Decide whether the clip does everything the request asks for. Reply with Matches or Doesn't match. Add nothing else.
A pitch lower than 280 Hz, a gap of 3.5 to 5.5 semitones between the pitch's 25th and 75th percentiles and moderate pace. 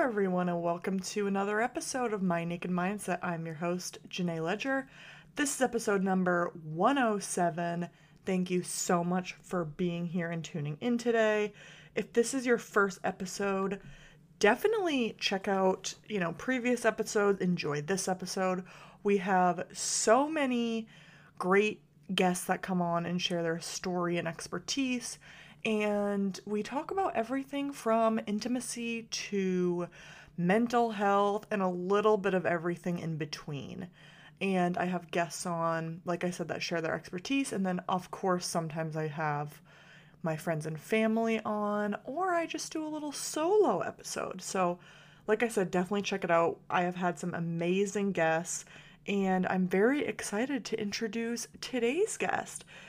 Matches